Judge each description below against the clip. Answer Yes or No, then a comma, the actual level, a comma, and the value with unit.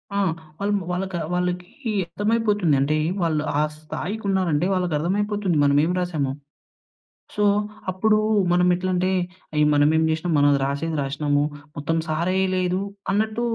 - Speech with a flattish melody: No, average, 4.0 semitones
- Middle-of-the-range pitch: Yes, medium, 180 Hz